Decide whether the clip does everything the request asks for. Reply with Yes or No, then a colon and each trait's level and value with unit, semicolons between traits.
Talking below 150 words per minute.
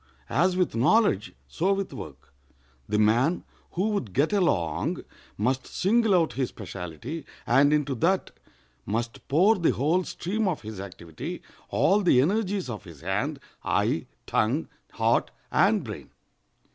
Yes: slow, 135 wpm